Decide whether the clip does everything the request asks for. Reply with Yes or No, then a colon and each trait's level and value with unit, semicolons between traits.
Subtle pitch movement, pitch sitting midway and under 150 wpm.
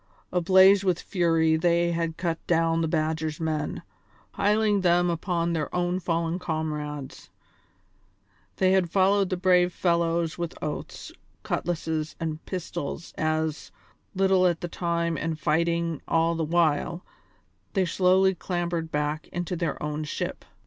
Yes: narrow, 2.1 semitones; medium, 170 Hz; slow, 135 wpm